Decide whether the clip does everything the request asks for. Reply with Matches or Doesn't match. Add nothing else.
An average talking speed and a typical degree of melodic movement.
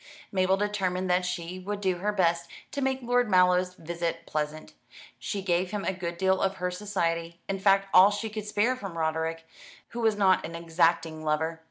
Matches